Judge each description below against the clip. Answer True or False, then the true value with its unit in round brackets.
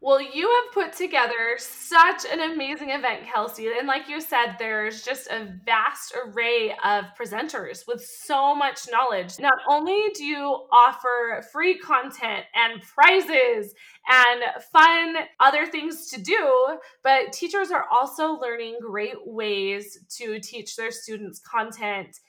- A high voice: True (255 Hz)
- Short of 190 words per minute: True (140 wpm)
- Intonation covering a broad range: True (5.9 semitones)